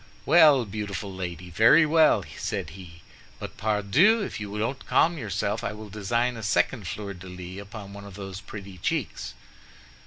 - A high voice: No, low, 105 Hz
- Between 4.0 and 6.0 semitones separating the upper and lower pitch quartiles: No, average, 3.5 semitones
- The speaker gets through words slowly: No, average, 165 wpm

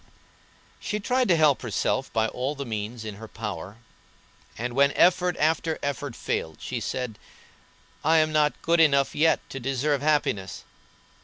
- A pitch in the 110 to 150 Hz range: Yes, medium, 140 Hz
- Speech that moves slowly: No, average, 155 wpm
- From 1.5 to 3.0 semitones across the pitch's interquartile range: No, wide, 5.5 semitones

